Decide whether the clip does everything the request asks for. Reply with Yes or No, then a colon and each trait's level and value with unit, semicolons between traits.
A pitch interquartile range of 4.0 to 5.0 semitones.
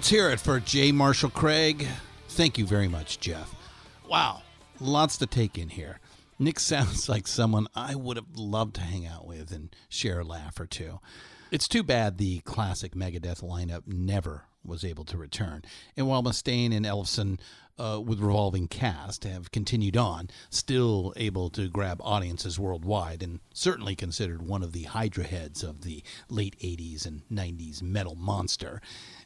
Yes: average, 4.3 semitones